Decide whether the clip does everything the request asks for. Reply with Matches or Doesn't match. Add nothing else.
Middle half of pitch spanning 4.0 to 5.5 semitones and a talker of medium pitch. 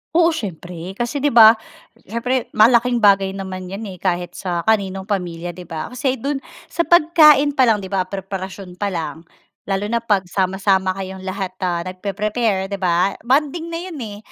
Doesn't match